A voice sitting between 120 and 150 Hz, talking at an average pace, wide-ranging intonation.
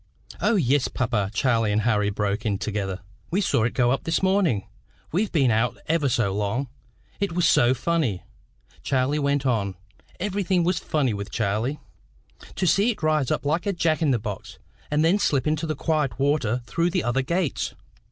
Yes: low, 135 Hz; average, 185 wpm; wide, 6.8 semitones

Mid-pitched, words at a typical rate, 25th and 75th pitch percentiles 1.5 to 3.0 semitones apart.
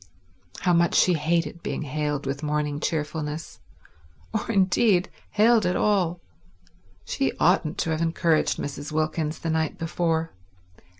No: medium, 160 Hz; slow, 125 wpm; narrow, 2.6 semitones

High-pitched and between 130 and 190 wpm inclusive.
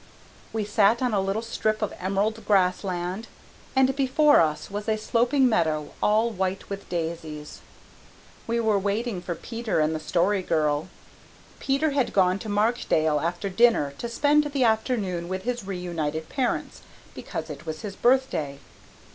Yes: high, 200 Hz; average, 155 wpm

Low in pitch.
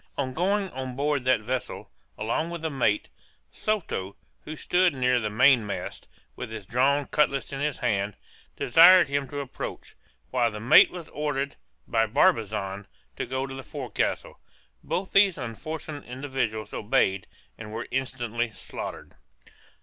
Yes: low, 130 Hz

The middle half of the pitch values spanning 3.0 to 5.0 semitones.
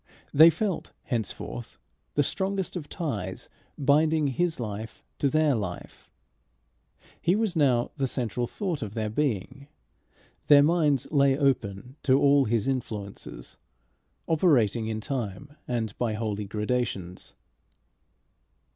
No: wide, 5.6 semitones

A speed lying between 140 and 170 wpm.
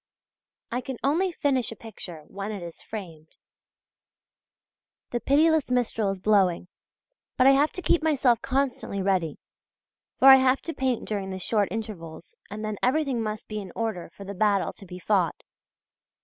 Yes: average, 165 wpm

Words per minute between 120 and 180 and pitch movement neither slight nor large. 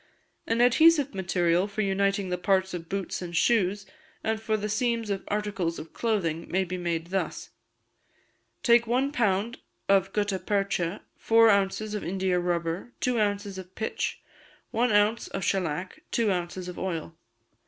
Yes: average, 155 wpm; average, 3.4 semitones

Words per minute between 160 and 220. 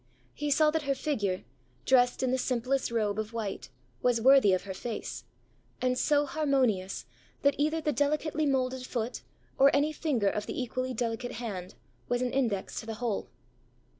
Yes: average, 170 wpm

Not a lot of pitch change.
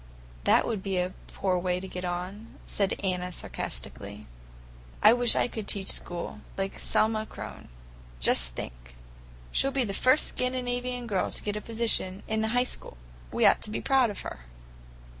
No: average, 4.5 semitones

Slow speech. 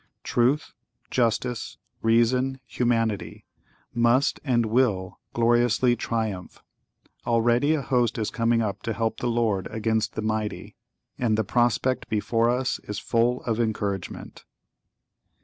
Yes: slow, 120 wpm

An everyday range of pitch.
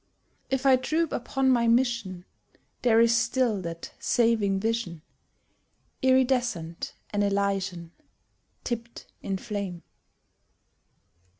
Yes: average, 4.3 semitones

